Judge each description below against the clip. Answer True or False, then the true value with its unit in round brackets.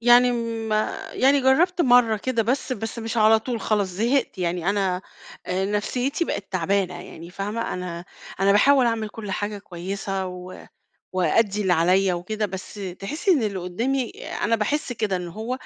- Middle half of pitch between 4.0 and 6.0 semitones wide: True (4.4 semitones)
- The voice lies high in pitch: True (210 Hz)